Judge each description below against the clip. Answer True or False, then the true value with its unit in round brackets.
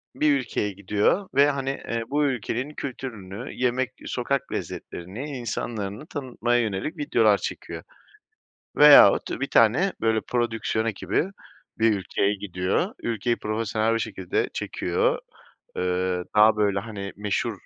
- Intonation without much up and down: False (4.3 semitones)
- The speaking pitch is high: False (115 Hz)